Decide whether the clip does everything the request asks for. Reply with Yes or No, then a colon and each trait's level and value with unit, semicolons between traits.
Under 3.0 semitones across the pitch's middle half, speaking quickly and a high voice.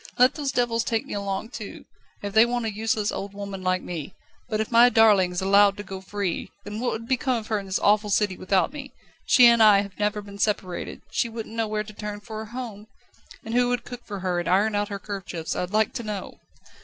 Yes: narrow, 2.5 semitones; fast, 240 wpm; high, 210 Hz